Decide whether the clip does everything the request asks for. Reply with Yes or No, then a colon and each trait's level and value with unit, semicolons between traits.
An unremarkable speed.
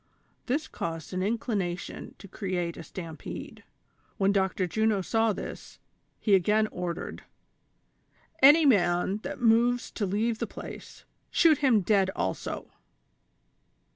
No: slow, 125 wpm